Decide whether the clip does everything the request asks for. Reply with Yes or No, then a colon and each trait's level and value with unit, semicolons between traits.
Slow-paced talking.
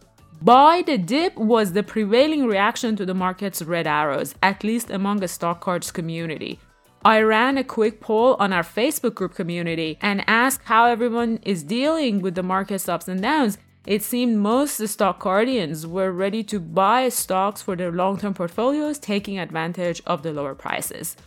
No: average, 175 wpm